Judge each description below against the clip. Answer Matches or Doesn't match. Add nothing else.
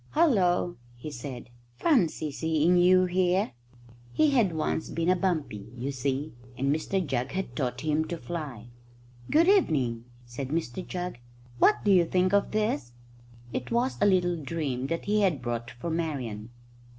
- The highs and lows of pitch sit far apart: Matches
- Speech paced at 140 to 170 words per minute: Matches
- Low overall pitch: Doesn't match